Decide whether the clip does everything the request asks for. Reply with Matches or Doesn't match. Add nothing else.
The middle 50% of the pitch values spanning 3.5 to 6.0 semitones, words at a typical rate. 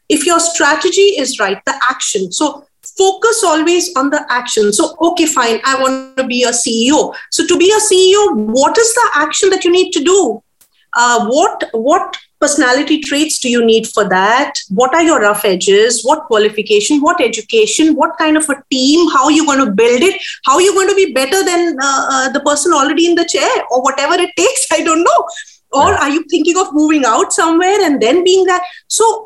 Doesn't match